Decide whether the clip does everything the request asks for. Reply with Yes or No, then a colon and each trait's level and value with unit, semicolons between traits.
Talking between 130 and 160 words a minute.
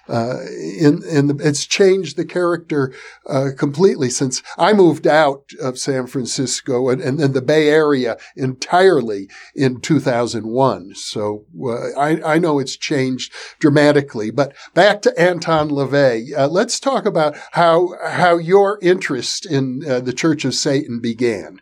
Yes: average, 150 wpm